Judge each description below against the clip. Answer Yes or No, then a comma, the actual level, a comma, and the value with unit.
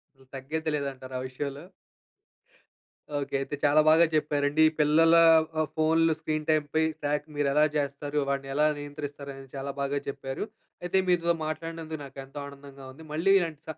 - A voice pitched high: No, medium, 145 Hz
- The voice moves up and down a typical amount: No, narrow, 2.1 semitones